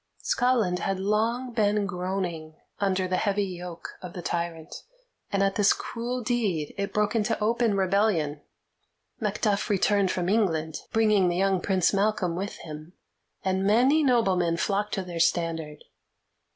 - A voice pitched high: Yes, high, 195 Hz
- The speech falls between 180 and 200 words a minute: No, average, 145 wpm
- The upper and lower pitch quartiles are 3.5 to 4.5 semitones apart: No, average, 3.1 semitones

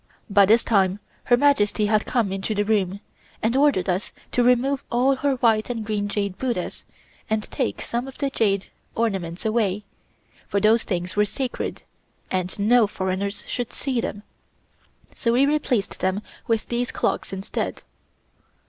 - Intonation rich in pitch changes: No, average, 3.6 semitones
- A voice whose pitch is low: No, high, 215 Hz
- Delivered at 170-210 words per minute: No, average, 155 wpm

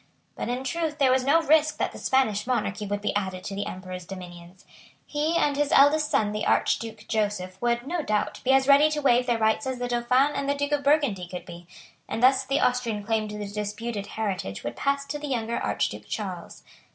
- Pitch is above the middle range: Yes, high, 240 Hz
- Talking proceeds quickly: Yes, fast, 220 wpm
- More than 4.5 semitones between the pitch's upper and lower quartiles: Yes, wide, 5.5 semitones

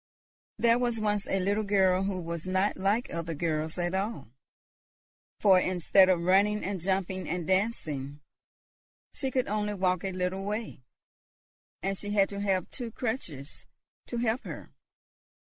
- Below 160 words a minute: Yes, average, 150 wpm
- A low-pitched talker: No, high, 195 Hz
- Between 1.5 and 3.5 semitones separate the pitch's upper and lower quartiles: Yes, narrow, 2.5 semitones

